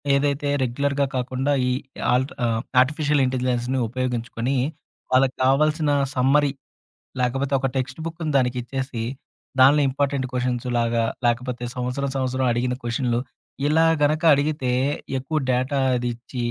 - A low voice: Yes, low, 130 Hz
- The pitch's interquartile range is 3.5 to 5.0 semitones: No, narrow, 2.4 semitones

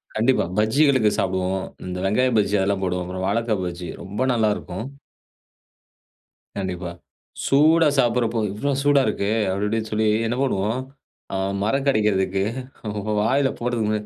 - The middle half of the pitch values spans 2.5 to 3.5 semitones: No, average, 4.3 semitones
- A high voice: No, low, 110 Hz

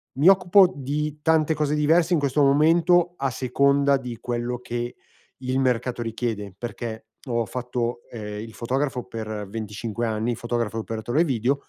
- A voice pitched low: Yes, low, 125 Hz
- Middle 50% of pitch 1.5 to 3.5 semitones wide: No, average, 4.2 semitones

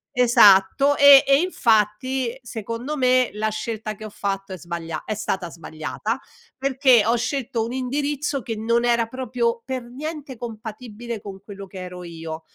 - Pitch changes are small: No, average, 4.2 semitones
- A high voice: Yes, high, 230 Hz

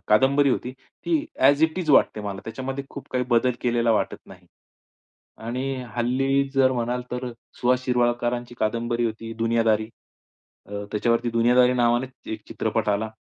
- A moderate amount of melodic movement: No, narrow, 2.2 semitones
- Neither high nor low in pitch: No, low, 120 Hz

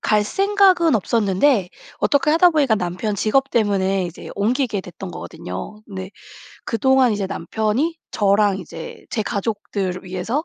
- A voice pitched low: No, high, 210 Hz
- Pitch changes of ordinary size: No, wide, 5.7 semitones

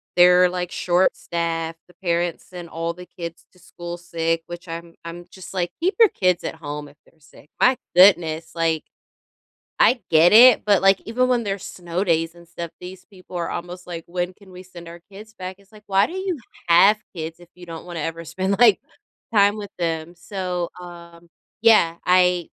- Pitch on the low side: No, medium, 175 Hz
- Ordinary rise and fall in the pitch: No, narrow, 2.3 semitones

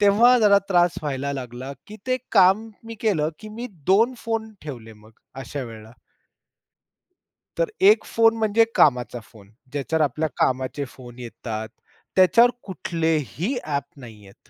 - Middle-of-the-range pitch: Yes, medium, 155 Hz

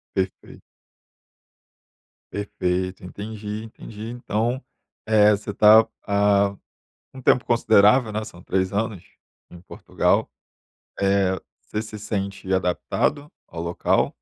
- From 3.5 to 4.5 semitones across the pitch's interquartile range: No, narrow, 2.4 semitones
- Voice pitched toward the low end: Yes, low, 105 Hz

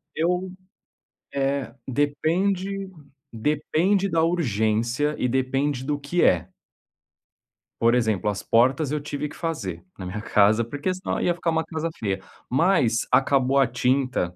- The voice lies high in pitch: No, medium, 140 Hz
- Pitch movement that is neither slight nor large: No, wide, 5.8 semitones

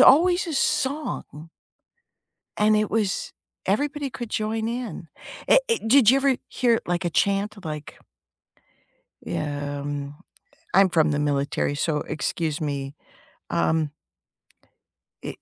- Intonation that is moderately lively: No, wide, 8.6 semitones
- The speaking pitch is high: Yes, high, 195 Hz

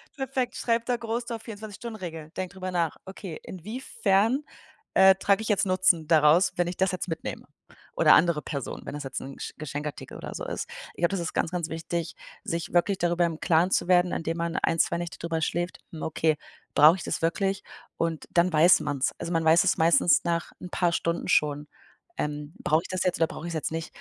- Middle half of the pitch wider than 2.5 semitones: Yes, average, 2.9 semitones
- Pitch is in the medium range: Yes, medium, 170 Hz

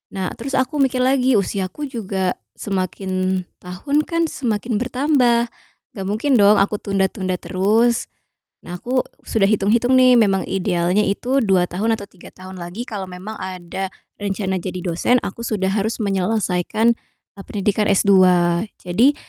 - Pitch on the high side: Yes, high, 205 Hz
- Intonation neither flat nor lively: Yes, average, 4.2 semitones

